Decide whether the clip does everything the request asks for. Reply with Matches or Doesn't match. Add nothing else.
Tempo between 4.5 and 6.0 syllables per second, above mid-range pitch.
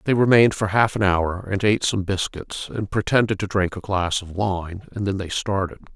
Doesn't match